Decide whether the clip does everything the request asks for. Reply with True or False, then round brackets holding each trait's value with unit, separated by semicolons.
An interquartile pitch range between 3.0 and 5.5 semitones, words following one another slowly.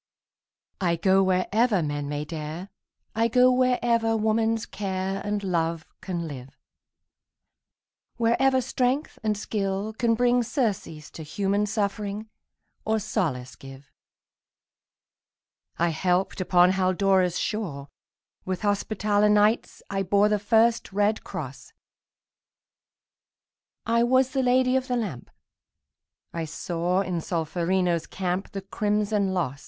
True (4.1 semitones; 115 wpm)